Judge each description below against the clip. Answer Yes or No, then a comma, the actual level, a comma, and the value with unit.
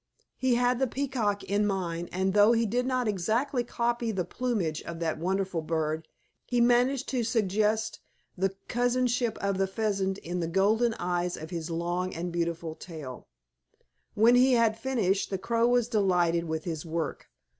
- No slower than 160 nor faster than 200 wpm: Yes, average, 165 wpm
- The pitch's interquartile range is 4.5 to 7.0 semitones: Yes, wide, 5.6 semitones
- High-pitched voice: Yes, high, 200 Hz